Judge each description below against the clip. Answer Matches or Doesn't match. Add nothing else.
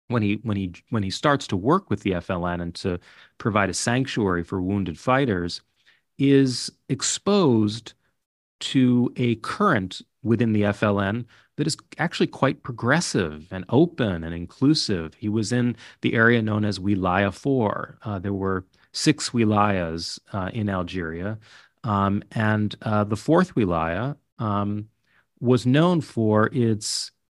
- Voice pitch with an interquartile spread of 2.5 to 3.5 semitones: Doesn't match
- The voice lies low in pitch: Matches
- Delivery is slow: Doesn't match